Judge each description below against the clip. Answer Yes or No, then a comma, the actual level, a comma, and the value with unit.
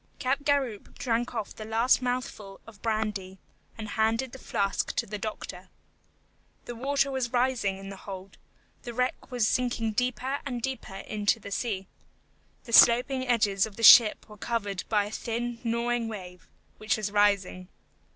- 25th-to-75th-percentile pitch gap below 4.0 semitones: Yes, average, 3.2 semitones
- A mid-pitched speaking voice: No, high, 225 Hz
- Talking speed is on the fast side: No, average, 160 wpm